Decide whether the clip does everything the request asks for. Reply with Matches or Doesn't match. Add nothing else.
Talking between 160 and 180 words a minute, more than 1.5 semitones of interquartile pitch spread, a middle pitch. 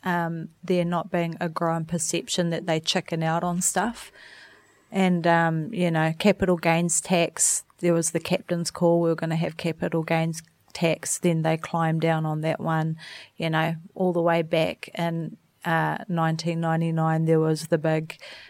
Doesn't match